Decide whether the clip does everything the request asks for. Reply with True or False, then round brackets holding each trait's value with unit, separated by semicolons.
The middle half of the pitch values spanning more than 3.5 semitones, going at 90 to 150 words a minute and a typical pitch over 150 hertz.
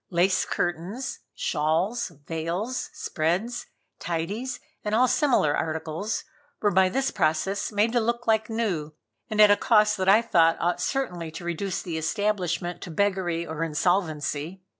True (4.6 semitones; 145 wpm; 185 Hz)